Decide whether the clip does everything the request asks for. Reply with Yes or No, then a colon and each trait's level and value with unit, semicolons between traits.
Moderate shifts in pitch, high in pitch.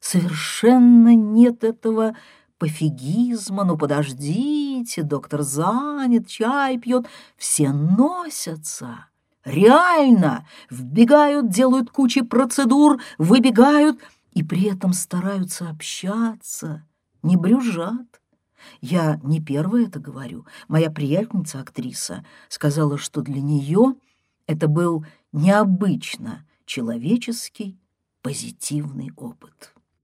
No: wide, 7.7 semitones; high, 195 Hz